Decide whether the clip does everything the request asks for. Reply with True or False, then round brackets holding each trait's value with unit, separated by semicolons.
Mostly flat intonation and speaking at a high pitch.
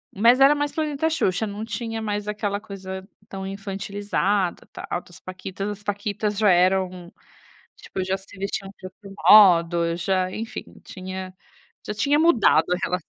True (2.2 semitones; 195 Hz)